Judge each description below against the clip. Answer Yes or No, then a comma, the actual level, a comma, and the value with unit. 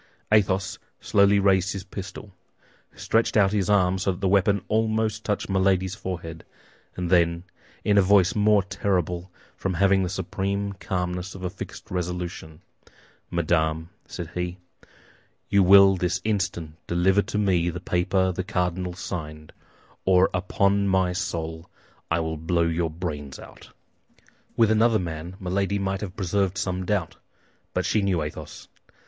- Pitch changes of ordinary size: No, narrow, 2.2 semitones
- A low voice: Yes, very low, 95 Hz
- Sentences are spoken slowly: No, average, 150 wpm